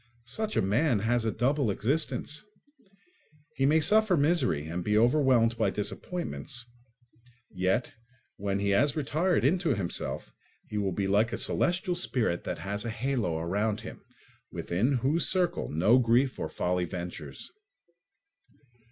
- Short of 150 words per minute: Yes, average, 140 wpm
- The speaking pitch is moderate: No, low, 120 Hz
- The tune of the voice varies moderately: No, wide, 6.9 semitones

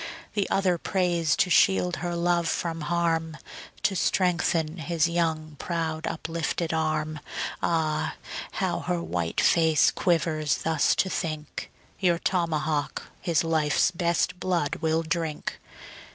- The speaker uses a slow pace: Yes, slow, 125 wpm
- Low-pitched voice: No, medium, 165 Hz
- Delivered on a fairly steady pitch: Yes, narrow, 1.8 semitones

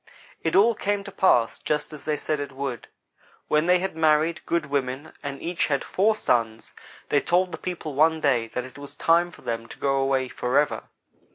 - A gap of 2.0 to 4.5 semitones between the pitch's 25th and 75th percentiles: Yes, average, 4.0 semitones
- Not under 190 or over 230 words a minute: Yes, average, 200 wpm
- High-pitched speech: No, medium, 150 Hz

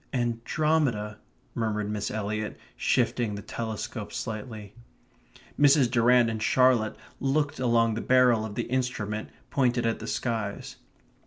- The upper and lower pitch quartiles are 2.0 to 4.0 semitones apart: Yes, average, 2.8 semitones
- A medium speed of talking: No, slow, 125 wpm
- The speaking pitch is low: Yes, low, 115 Hz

